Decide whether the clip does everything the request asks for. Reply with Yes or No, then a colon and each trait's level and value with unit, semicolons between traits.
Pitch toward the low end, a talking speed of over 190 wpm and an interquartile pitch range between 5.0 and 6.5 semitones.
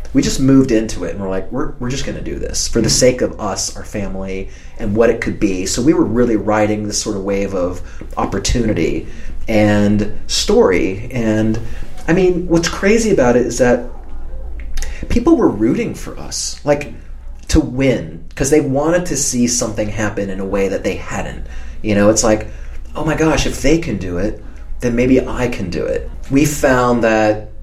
Yes: low, 105 Hz; average, 200 wpm; wide, 5.5 semitones